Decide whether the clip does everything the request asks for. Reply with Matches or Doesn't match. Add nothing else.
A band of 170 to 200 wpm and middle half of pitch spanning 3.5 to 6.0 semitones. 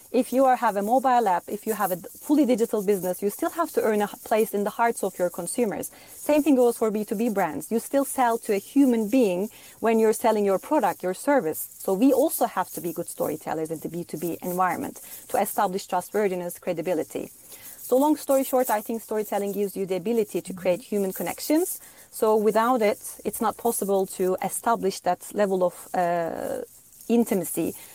Matches